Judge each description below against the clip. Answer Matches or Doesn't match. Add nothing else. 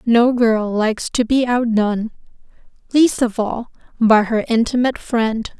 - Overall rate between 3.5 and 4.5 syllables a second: Matches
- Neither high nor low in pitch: Doesn't match